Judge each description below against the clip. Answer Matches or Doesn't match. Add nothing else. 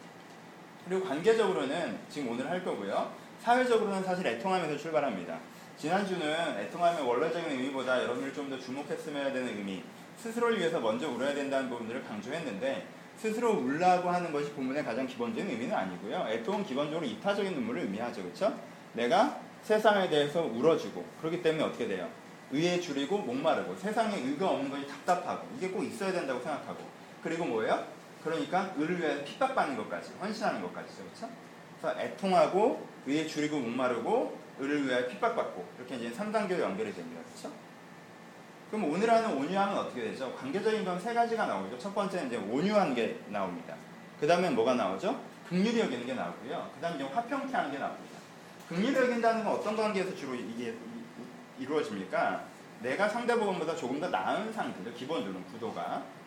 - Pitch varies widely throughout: Matches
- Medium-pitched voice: Matches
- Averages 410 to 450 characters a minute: Matches